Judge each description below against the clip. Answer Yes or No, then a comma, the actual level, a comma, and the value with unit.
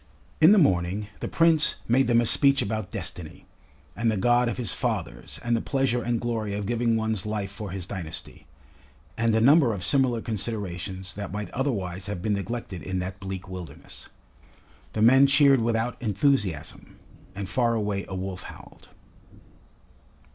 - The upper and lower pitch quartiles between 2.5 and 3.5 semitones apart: No, average, 3.9 semitones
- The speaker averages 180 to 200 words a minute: No, average, 165 wpm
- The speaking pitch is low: Yes, low, 110 Hz